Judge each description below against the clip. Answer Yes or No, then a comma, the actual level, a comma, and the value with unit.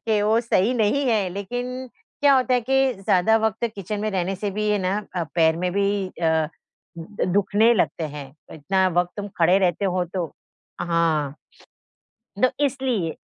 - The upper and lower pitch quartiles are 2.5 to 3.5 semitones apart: No, average, 3.9 semitones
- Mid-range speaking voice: No, high, 200 Hz